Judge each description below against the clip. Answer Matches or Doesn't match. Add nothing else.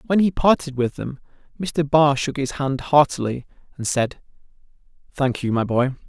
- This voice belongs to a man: Matches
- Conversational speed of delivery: Matches